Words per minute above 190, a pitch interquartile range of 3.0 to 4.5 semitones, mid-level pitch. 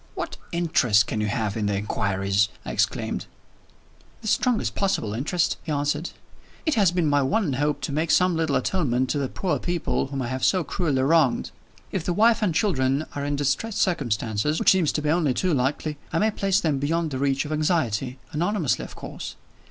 No: average, 200 wpm; average, 5.0 semitones; medium, 150 Hz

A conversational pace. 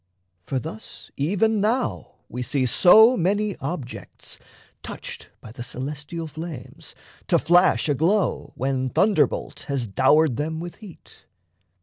No: slow, 120 wpm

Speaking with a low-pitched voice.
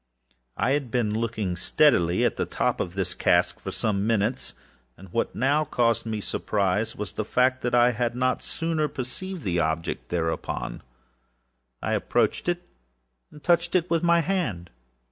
Yes: low, 120 Hz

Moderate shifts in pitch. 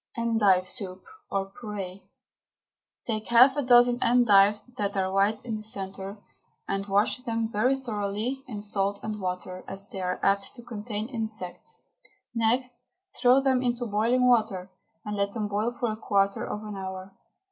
Yes: average, 3.4 semitones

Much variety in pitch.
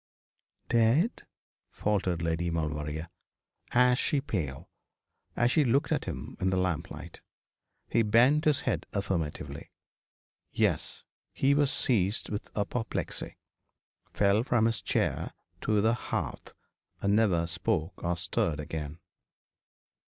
Yes: wide, 6.0 semitones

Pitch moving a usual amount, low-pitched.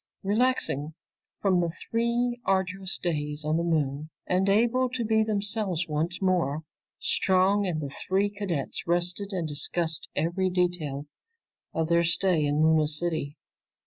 No: average, 4.2 semitones; medium, 175 Hz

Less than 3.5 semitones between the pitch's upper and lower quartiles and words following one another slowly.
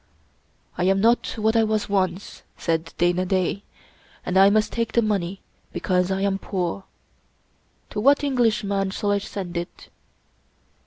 No: average, 2.7 semitones; average, 165 wpm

